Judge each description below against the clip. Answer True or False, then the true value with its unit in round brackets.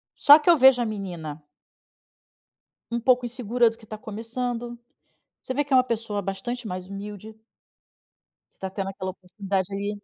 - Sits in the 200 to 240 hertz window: True (220 Hz)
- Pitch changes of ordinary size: True (3.9 semitones)